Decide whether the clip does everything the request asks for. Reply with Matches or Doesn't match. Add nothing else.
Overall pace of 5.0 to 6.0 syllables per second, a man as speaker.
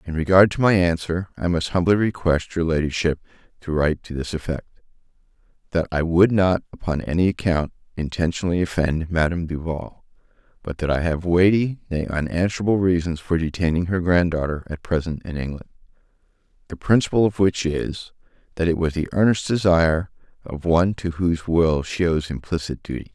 Matches